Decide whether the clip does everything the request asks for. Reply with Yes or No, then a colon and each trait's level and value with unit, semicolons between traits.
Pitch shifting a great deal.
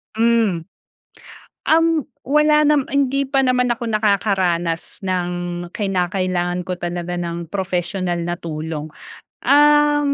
Yes: wide, 7.5 semitones